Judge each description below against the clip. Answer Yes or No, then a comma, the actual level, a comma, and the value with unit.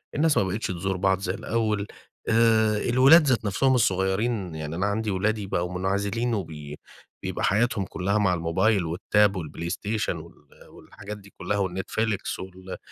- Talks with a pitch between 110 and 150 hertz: No, low, 100 Hz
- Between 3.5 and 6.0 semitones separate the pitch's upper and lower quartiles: No, average, 2.9 semitones